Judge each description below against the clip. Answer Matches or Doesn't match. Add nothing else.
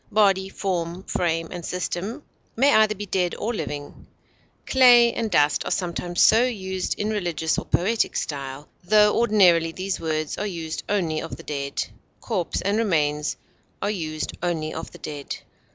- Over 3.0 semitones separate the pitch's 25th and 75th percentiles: Matches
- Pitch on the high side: Doesn't match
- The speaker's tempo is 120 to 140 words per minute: Doesn't match